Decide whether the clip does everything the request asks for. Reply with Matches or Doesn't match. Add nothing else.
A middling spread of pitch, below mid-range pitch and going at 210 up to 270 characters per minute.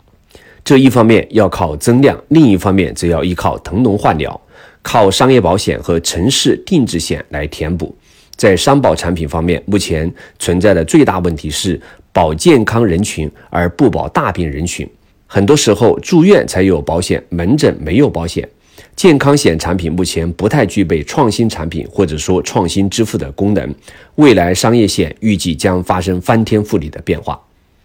Matches